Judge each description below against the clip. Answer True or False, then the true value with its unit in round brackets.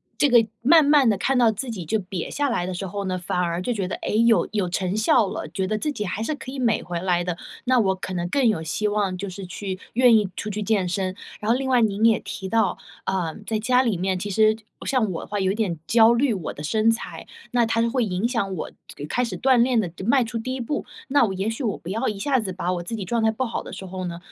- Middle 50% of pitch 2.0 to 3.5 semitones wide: False (4.1 semitones)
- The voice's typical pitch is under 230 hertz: True (215 Hz)